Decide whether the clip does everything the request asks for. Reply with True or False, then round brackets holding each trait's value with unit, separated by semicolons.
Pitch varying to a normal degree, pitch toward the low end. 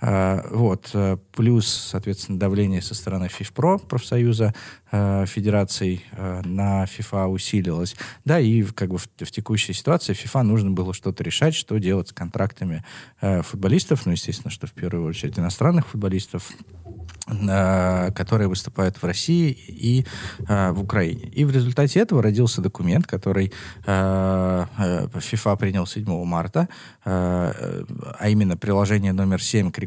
True (3.2 semitones; 100 Hz)